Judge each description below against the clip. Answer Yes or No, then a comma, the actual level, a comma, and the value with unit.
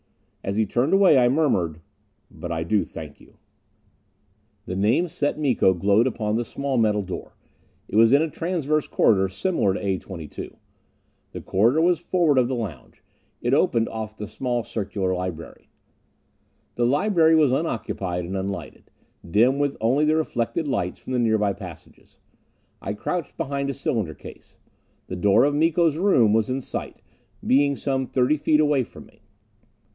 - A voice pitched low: Yes, low, 120 Hz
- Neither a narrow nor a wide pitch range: No, wide, 6.5 semitones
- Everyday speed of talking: Yes, average, 165 wpm